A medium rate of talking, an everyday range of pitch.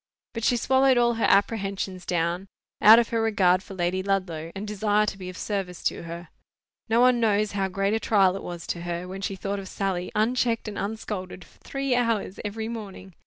No: fast, 210 wpm; average, 3.3 semitones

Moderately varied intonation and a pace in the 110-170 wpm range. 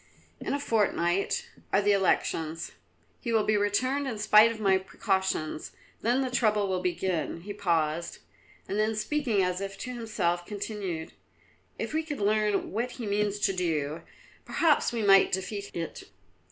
Yes: average, 3.5 semitones; average, 160 wpm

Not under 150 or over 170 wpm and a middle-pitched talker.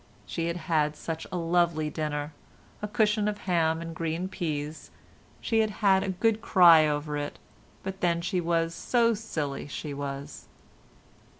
Yes: average, 155 wpm; medium, 165 Hz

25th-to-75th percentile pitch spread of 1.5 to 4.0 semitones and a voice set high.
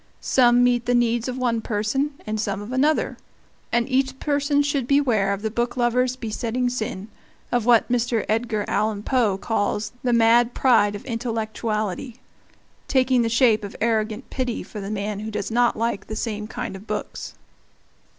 Yes: narrow, 2.6 semitones; high, 235 Hz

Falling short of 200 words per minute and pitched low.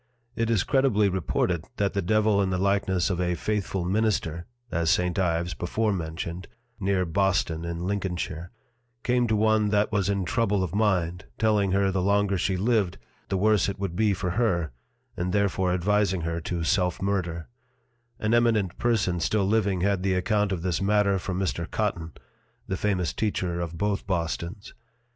Yes: average, 170 wpm; very low, 95 Hz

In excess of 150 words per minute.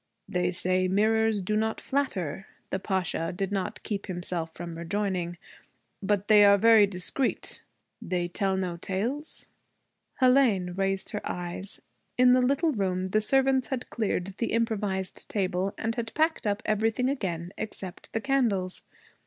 No: average, 145 wpm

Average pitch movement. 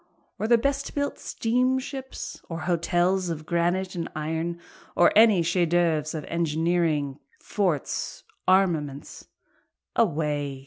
Yes: average, 3.5 semitones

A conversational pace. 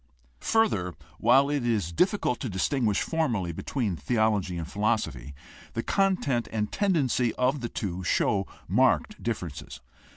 No: slow, 130 wpm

